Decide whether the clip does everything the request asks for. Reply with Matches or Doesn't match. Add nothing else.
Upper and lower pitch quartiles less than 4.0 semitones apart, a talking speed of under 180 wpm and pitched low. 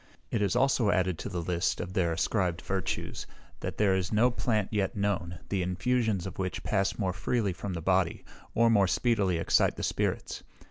Doesn't match